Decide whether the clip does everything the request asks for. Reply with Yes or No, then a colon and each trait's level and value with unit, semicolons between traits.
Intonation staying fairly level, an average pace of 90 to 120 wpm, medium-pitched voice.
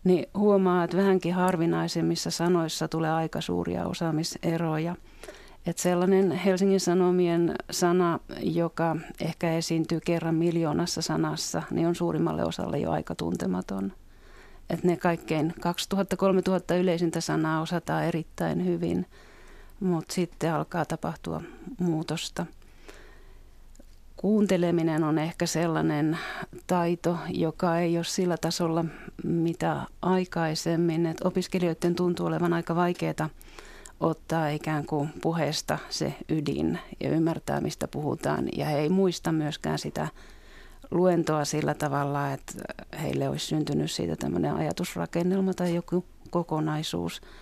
Yes: narrow, 2.2 semitones; average, 115 wpm; medium, 170 Hz